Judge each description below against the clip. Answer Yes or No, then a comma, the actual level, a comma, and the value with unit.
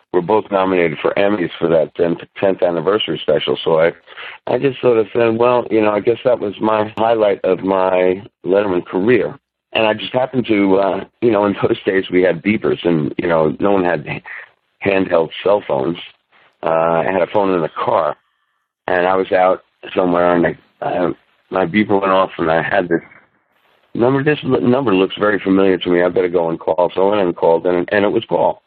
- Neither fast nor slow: No, fast, 210 wpm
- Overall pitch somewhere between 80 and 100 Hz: Yes, very low, 95 Hz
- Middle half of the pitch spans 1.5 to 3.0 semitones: No, average, 3.7 semitones